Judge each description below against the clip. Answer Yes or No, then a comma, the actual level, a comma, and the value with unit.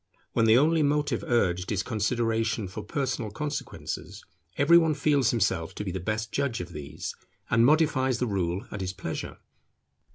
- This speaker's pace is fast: No, average, 165 wpm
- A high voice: No, low, 115 Hz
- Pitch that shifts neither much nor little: No, wide, 6.5 semitones